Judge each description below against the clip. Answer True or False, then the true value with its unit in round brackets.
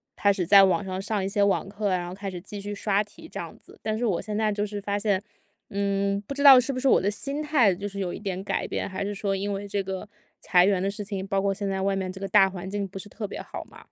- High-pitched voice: True (200 Hz)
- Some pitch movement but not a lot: False (1.3 semitones)